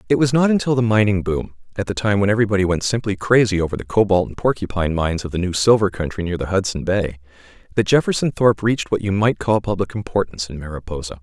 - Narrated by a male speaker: Yes, male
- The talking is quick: Yes, fast, 225 wpm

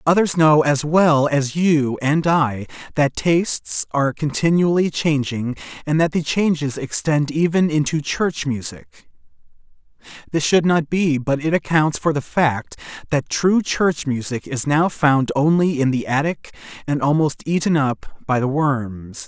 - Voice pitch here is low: No, medium, 150 Hz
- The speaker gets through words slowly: No, average, 155 wpm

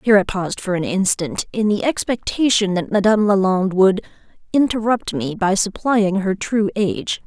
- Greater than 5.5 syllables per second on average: No, 5.3 syllables/s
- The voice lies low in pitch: No, high, 200 Hz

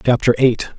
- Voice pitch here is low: Yes, low, 120 Hz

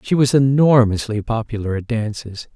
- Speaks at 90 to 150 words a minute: Yes, average, 140 wpm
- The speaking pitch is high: No, low, 120 Hz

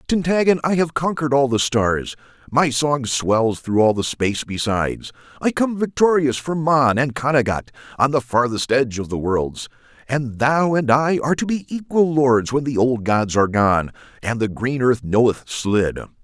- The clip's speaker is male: Yes, male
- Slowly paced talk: No, average, 185 wpm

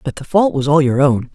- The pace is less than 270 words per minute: No, fast, 315 wpm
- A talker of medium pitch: Yes, medium, 150 Hz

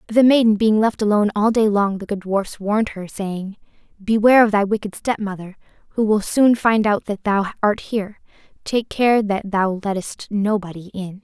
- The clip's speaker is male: No, female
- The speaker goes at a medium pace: Yes, average, 185 wpm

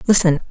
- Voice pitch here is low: No, medium, 175 Hz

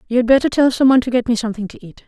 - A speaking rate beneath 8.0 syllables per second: No, 8.6 syllables/s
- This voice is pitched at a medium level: No, high, 240 Hz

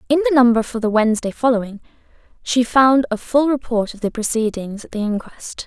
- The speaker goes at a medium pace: Yes, average, 190 wpm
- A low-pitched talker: No, high, 240 Hz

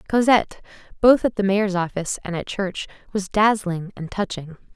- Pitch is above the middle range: Yes, high, 195 Hz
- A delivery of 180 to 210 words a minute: No, average, 165 wpm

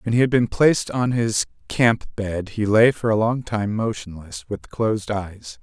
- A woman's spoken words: No, male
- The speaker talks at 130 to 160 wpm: No, fast, 205 wpm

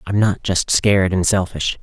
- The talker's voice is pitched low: Yes, very low, 95 Hz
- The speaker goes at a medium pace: Yes, average, 195 wpm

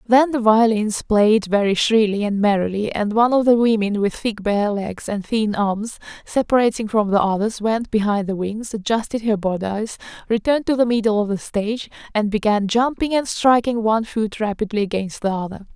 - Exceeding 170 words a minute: Yes, average, 185 wpm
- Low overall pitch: No, high, 215 Hz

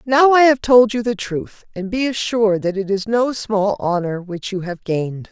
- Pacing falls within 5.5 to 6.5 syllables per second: No, 4.7 syllables/s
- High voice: Yes, high, 210 Hz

